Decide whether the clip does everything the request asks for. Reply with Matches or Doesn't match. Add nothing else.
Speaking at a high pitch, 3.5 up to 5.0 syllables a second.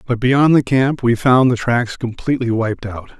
Doesn't match